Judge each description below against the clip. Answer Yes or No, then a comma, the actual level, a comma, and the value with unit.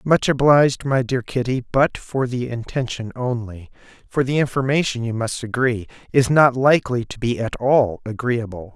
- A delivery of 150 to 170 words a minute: Yes, average, 160 wpm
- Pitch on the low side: Yes, low, 125 Hz